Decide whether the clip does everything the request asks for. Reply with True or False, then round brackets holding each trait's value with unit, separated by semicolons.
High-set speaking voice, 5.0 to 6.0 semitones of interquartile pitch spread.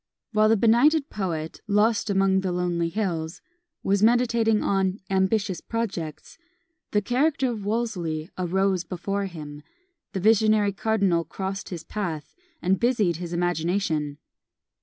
False (195 Hz; 4.0 semitones)